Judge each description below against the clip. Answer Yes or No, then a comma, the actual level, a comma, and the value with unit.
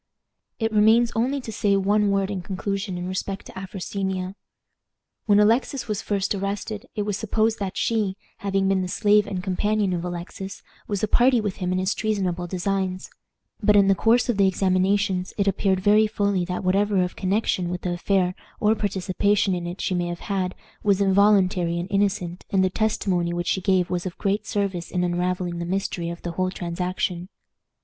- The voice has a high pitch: Yes, high, 195 Hz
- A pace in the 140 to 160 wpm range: No, average, 190 wpm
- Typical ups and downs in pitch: No, narrow, 2.1 semitones